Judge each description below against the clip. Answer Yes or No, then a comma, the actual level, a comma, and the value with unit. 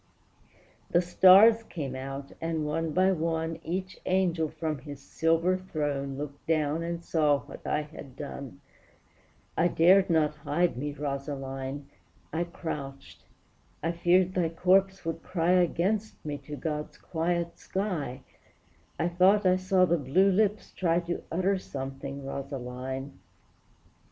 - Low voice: No, medium, 165 Hz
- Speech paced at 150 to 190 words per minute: No, slow, 135 wpm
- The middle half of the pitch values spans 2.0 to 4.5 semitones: Yes, average, 4.2 semitones